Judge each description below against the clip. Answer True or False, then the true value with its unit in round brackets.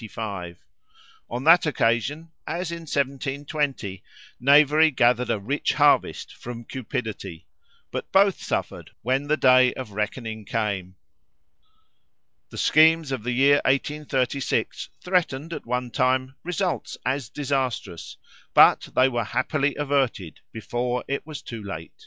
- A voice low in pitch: True (130 Hz)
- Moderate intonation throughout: True (3.9 semitones)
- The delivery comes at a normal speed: False (120 wpm)